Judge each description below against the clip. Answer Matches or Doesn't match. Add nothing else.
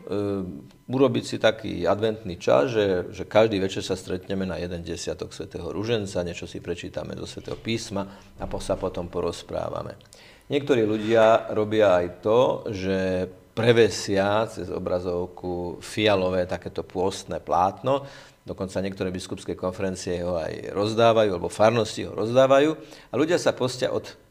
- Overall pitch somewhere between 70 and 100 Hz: Matches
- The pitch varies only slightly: Doesn't match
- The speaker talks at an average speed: Matches